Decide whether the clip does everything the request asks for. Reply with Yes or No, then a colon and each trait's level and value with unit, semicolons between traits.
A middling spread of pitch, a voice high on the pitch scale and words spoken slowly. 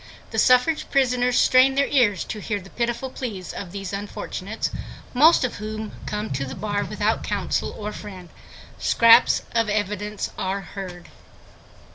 No: average, 3.9 semitones; high, 210 Hz; average, 150 wpm